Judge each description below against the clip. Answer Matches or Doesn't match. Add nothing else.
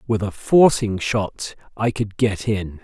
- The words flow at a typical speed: Matches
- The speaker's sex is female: Doesn't match